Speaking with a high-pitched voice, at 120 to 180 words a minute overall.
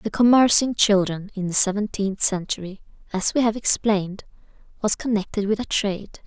Yes: high, 205 Hz; average, 165 wpm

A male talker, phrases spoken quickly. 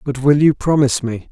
Yes: male; fast, 225 wpm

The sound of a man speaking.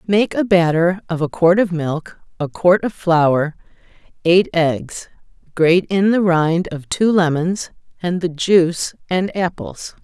No: female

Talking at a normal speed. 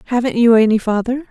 Yes: average, 185 wpm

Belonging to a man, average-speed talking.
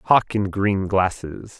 Yes: male; average, 150 wpm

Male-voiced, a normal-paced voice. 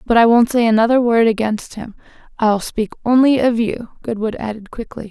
No: female; average, 190 wpm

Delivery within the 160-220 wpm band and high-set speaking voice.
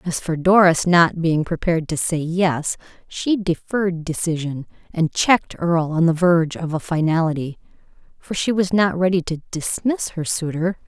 No: average, 165 wpm; medium, 170 Hz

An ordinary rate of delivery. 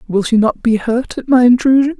No: fast, 240 wpm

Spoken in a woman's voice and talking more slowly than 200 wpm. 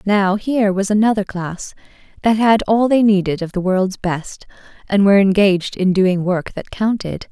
Yes: female; average, 180 wpm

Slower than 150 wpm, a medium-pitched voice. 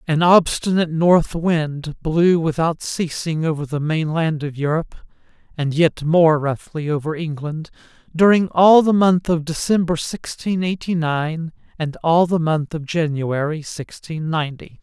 Yes: average, 140 wpm; medium, 160 Hz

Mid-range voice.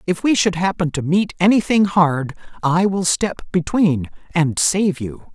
Yes: medium, 180 Hz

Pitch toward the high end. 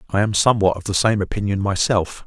No: low, 100 Hz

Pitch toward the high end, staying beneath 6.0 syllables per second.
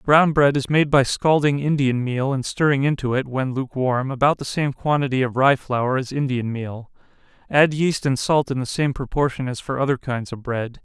No: low, 135 Hz; 5.0 syllables/s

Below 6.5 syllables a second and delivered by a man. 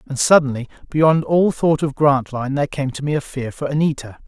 Yes: 5.7 syllables/s; male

